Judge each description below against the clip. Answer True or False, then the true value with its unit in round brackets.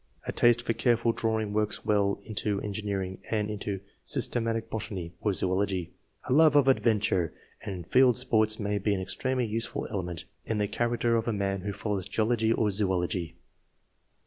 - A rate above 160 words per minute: True (170 wpm)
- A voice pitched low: True (105 Hz)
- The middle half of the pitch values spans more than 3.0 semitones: False (2.7 semitones)